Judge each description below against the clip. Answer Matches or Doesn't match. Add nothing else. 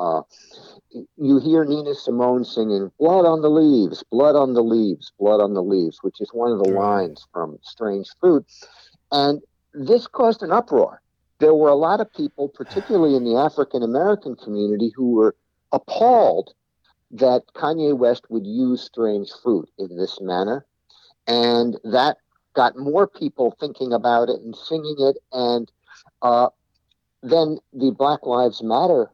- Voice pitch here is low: Matches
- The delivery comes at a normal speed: Matches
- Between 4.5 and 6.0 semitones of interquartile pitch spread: Matches